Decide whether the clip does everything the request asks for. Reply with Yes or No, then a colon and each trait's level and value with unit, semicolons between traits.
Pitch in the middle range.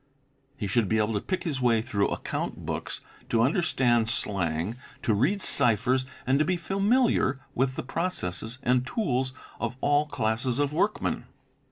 No: low, 125 Hz